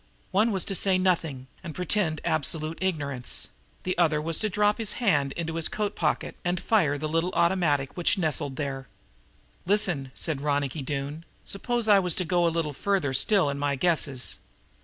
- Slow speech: No, average, 180 wpm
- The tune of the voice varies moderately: Yes, average, 4.6 semitones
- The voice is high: No, medium, 165 Hz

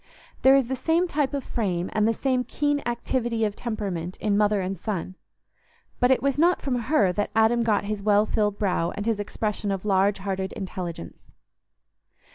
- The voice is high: Yes, high, 215 Hz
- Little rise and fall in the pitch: No, average, 4.1 semitones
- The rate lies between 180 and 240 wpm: Yes, average, 185 wpm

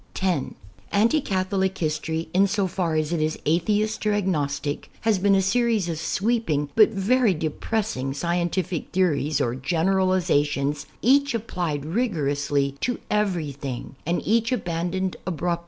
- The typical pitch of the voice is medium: Yes, medium, 180 Hz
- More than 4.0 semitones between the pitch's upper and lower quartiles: Yes, average, 5.1 semitones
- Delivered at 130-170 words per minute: Yes, average, 140 wpm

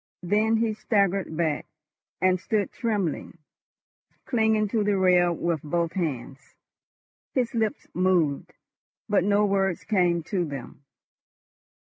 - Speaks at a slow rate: Yes, slow, 115 wpm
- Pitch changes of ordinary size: Yes, average, 3.8 semitones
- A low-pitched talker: No, medium, 185 Hz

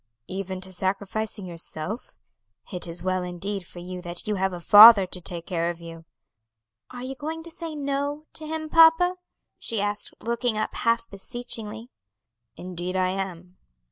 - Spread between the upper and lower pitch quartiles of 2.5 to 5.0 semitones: No, wide, 5.4 semitones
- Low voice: No, high, 200 Hz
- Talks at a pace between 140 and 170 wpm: Yes, average, 165 wpm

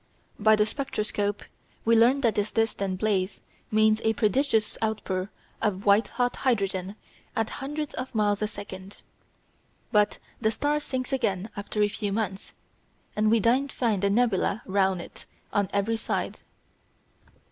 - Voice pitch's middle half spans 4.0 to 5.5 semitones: No, narrow, 2.4 semitones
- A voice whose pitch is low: No, high, 215 Hz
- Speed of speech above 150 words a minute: No, average, 145 wpm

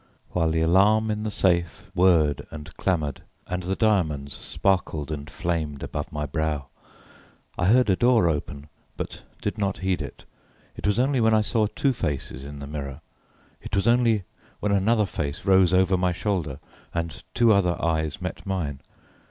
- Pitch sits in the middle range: No, very low, 90 Hz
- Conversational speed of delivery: Yes, average, 170 wpm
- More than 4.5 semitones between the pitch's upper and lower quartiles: Yes, wide, 5.4 semitones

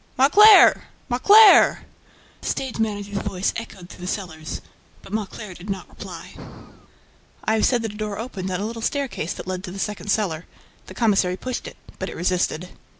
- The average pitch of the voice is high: Yes, high, 205 Hz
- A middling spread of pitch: Yes, average, 3.8 semitones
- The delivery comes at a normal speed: Yes, average, 180 wpm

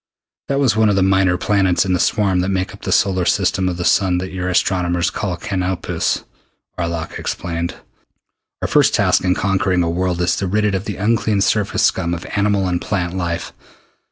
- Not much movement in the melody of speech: Yes, narrow, 2.0 semitones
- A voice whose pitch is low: Yes, very low, 95 Hz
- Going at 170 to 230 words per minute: Yes, average, 200 wpm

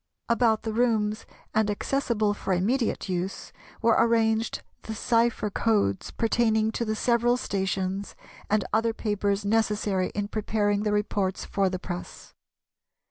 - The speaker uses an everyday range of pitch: No, narrow, 2.1 semitones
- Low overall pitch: No, high, 215 Hz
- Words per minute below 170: Yes, slow, 135 wpm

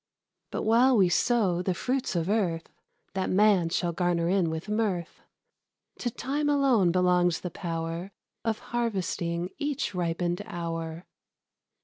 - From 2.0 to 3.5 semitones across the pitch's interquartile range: No, average, 4.4 semitones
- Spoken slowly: Yes, slow, 130 wpm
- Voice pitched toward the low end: No, medium, 180 Hz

